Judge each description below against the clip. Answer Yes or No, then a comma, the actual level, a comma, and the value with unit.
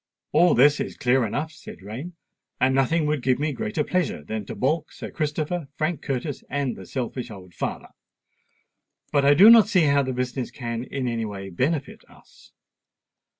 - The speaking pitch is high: No, medium, 140 Hz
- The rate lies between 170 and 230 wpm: Yes, average, 180 wpm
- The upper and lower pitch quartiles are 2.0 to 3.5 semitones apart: No, average, 4.0 semitones